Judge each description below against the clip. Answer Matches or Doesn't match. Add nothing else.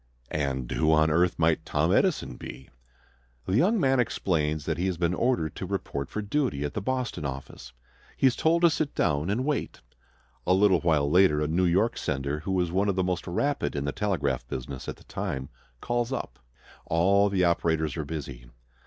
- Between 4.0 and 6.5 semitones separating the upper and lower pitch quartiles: Matches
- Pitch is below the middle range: Matches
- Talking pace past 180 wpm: Matches